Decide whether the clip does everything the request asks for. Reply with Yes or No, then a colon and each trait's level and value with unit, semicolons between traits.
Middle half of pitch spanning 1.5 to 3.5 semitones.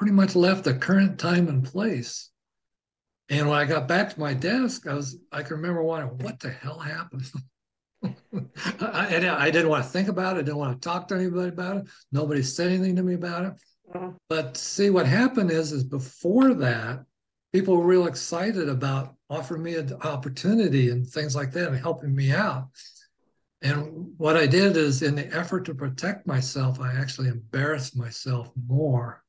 No: average, 5.0 semitones